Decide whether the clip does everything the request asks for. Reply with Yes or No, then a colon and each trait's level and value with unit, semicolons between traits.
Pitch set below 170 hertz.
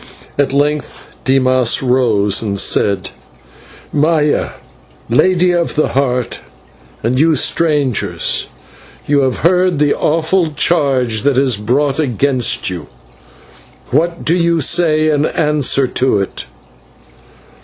Yes: medium, 140 Hz